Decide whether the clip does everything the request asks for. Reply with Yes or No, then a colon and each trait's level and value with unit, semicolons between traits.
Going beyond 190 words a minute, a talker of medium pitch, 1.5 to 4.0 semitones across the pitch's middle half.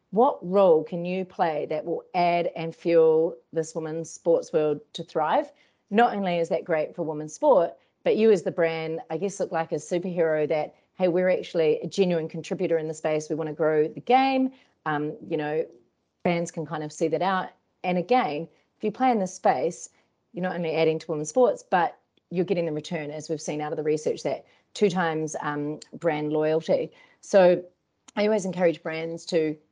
Yes: average, 200 wpm; medium, 165 Hz; average, 2.9 semitones